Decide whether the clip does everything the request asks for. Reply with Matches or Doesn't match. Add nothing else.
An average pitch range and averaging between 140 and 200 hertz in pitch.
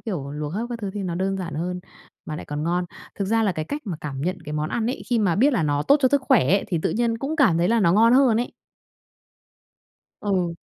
Doesn't match